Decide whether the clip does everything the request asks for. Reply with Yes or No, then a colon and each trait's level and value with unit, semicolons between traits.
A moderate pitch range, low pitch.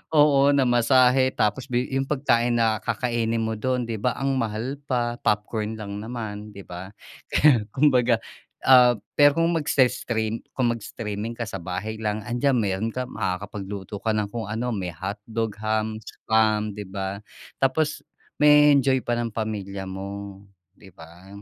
Yes: average, 3.5 semitones; low, 115 Hz